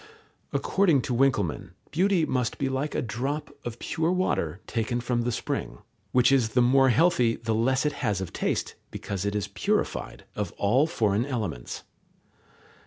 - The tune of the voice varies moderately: Yes, average, 4.0 semitones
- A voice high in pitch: No, low, 125 Hz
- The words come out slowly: No, average, 165 wpm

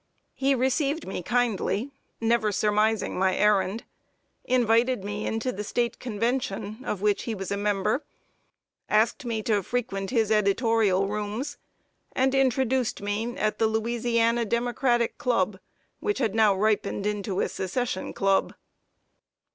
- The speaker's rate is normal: No, slow, 130 wpm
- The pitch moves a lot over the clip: No, average, 3.0 semitones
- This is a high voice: Yes, high, 220 Hz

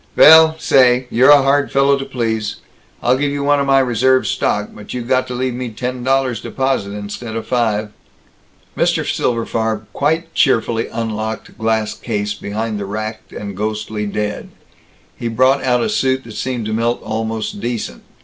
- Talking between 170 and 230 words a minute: Yes, average, 175 wpm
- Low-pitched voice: Yes, low, 120 Hz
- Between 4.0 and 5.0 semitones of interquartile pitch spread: No, average, 3.3 semitones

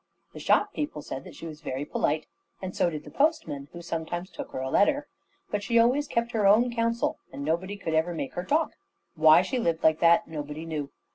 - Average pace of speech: No, fast, 220 wpm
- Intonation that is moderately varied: No, wide, 6.8 semitones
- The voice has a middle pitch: Yes, medium, 170 Hz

